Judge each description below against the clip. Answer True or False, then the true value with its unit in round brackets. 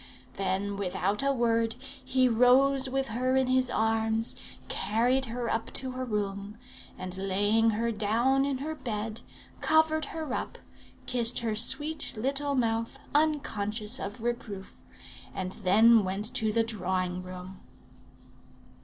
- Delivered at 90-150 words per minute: True (135 wpm)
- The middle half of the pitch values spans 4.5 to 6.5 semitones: False (4.0 semitones)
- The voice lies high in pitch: True (230 Hz)